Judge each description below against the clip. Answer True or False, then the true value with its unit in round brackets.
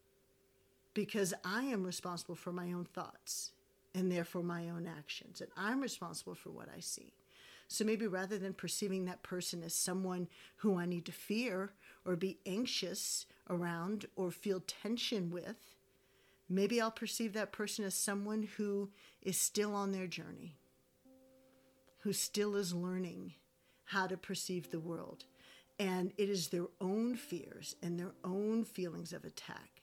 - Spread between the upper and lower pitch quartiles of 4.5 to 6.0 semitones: False (2.9 semitones)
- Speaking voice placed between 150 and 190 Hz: True (185 Hz)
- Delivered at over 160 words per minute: False (155 wpm)